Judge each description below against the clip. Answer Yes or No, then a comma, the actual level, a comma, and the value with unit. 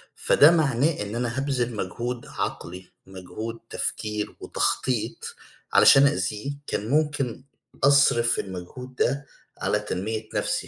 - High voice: No, low, 120 Hz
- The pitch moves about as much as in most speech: Yes, average, 4.7 semitones